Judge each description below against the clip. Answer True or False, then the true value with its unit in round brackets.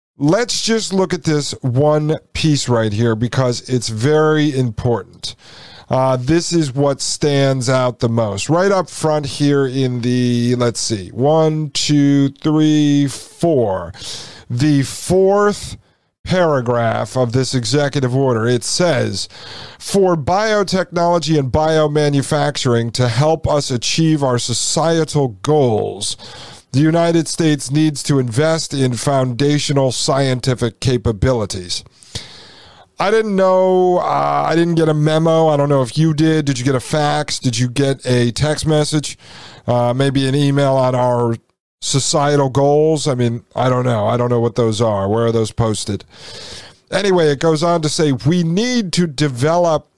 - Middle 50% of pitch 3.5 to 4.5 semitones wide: True (4.2 semitones)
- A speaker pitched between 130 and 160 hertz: True (140 Hz)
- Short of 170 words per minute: True (145 wpm)